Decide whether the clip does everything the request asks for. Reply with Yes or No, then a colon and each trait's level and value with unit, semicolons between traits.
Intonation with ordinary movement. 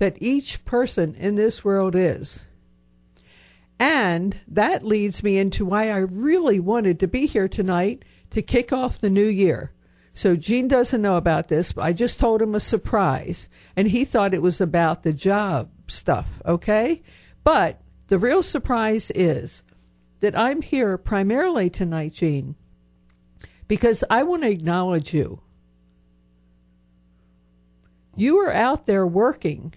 No: wide, 7.5 semitones